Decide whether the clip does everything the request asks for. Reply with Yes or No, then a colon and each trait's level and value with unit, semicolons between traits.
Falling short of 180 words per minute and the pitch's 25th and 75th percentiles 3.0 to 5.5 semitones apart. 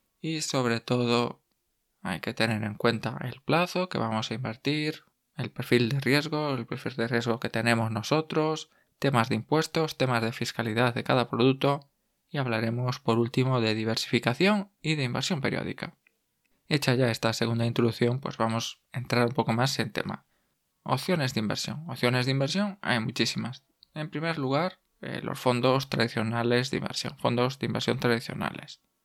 Yes: average, 160 wpm; average, 3.7 semitones